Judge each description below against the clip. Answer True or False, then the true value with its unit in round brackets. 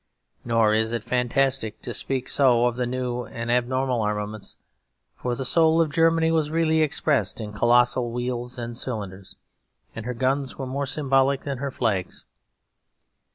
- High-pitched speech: False (125 Hz)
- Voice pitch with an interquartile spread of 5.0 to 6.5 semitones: False (2.8 semitones)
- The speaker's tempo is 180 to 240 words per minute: False (155 wpm)